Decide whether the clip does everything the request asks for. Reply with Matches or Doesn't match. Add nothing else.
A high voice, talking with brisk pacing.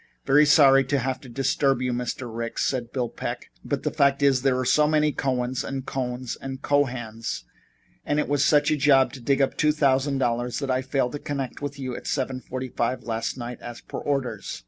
Doesn't match